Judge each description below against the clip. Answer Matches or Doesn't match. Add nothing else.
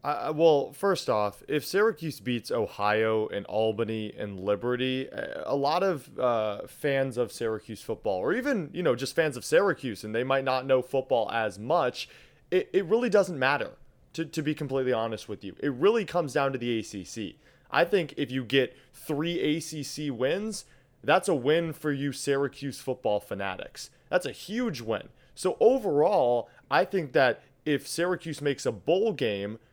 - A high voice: Doesn't match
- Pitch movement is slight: Doesn't match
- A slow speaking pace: Doesn't match